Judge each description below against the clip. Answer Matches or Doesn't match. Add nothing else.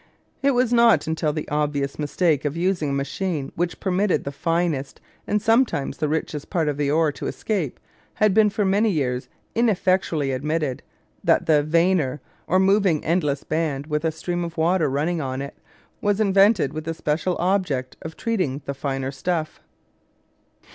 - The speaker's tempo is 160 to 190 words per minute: Matches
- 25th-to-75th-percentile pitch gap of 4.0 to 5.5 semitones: Matches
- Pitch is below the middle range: Doesn't match